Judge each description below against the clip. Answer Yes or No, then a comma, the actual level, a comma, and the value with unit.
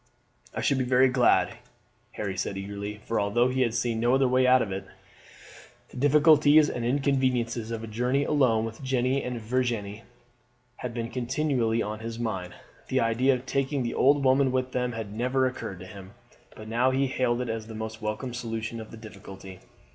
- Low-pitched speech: Yes, low, 120 Hz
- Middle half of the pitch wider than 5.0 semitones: No, average, 2.8 semitones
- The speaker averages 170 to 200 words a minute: Yes, average, 195 wpm